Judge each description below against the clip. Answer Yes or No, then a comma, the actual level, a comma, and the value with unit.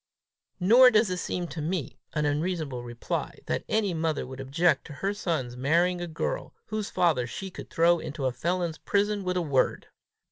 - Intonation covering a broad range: No, average, 4.2 semitones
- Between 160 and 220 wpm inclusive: Yes, average, 185 wpm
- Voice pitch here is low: No, medium, 170 Hz